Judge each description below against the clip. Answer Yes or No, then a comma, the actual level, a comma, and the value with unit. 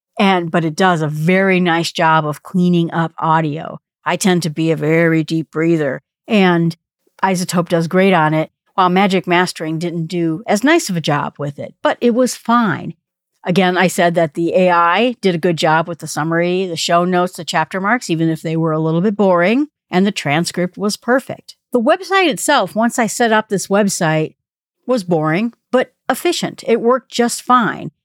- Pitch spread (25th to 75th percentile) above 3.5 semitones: Yes, average, 4.1 semitones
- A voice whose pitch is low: No, medium, 180 Hz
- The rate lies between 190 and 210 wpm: Yes, average, 195 wpm